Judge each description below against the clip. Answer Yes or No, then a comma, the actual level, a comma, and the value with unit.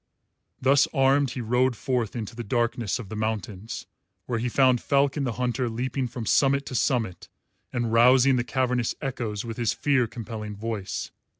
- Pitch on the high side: No, low, 120 Hz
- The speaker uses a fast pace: No, average, 170 wpm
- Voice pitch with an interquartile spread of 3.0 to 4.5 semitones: No, narrow, 2.5 semitones